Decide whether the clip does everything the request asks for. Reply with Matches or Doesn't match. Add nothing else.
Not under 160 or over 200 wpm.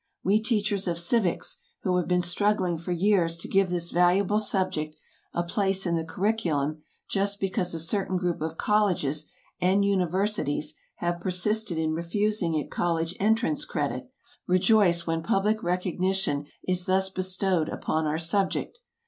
Doesn't match